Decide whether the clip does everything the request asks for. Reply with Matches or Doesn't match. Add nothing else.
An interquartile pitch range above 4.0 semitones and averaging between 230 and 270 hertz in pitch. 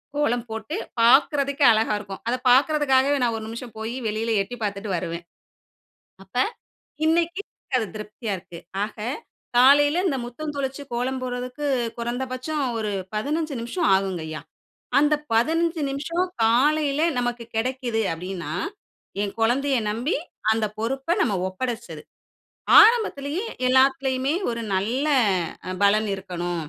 Matches